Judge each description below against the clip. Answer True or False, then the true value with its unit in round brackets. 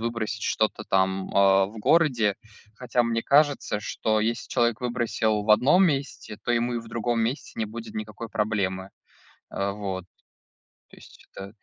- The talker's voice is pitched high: False (110 Hz)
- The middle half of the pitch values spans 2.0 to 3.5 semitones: True (2.5 semitones)